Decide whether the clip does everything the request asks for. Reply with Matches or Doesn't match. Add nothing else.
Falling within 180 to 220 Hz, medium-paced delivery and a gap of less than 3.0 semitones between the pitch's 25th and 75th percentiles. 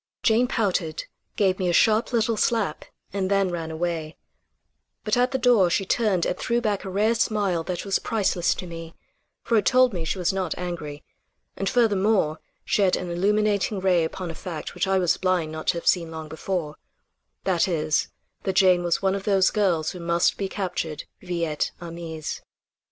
Doesn't match